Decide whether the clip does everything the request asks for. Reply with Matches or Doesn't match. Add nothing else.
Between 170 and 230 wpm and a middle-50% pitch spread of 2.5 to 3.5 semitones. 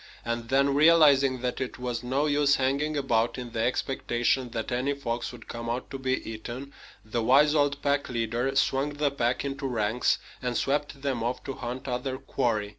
Matches